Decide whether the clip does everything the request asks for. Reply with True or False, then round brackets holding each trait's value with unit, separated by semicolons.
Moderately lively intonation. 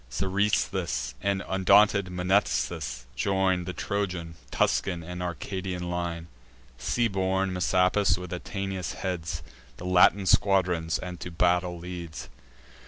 False (1.8 semitones)